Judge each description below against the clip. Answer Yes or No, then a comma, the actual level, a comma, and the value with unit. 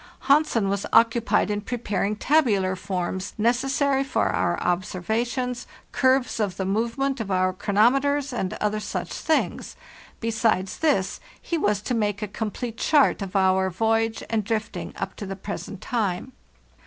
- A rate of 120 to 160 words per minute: Yes, average, 145 wpm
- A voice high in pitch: Yes, high, 220 Hz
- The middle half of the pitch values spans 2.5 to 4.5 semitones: Yes, average, 4.2 semitones